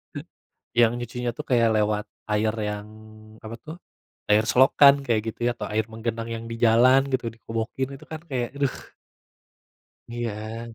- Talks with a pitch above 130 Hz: No, low, 115 Hz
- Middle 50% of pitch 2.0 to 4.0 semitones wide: Yes, narrow, 2.4 semitones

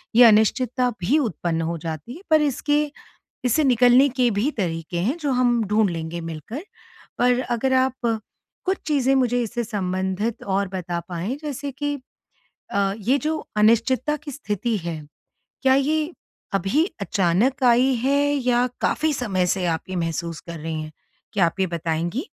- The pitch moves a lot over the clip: Yes, wide, 6.6 semitones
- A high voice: Yes, high, 235 Hz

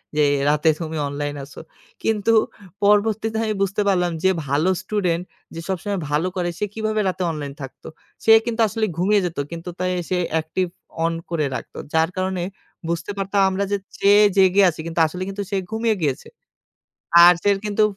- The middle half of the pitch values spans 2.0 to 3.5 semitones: No, average, 3.9 semitones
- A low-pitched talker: No, medium, 185 Hz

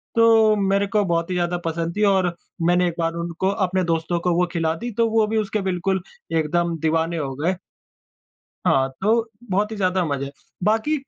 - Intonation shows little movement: No, average, 3.8 semitones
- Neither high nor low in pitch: Yes, medium, 180 Hz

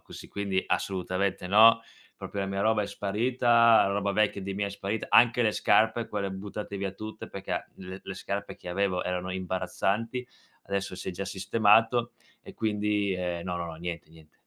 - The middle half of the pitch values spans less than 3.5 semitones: Yes, narrow, 2.6 semitones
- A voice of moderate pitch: No, low, 100 Hz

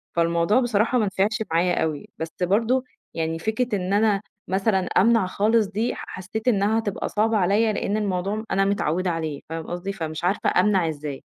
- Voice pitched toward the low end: No, high, 195 Hz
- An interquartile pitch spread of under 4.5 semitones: Yes, average, 4.1 semitones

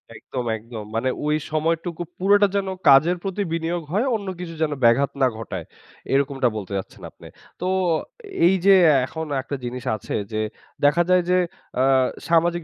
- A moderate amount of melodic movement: No, wide, 5.7 semitones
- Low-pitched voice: No, medium, 160 Hz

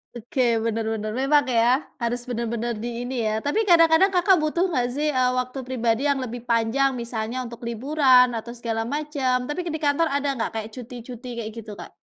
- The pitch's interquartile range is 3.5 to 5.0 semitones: Yes, average, 3.8 semitones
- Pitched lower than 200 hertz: No, very high, 250 Hz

